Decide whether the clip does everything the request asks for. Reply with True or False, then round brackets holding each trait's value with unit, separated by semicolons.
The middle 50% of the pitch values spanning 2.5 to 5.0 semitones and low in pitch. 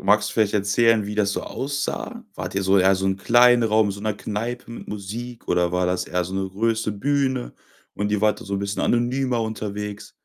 True (2.9 semitones; 105 Hz)